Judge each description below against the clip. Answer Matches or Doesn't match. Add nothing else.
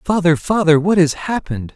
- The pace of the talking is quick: Doesn't match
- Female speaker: Doesn't match